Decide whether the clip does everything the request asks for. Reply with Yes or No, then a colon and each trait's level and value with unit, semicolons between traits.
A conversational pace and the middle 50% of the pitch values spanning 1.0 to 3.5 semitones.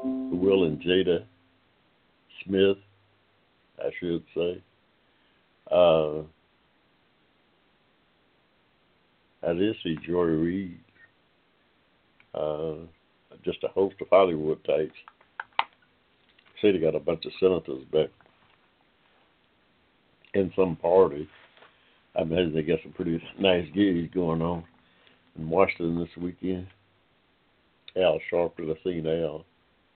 No: slow, 100 wpm; narrow, 2.5 semitones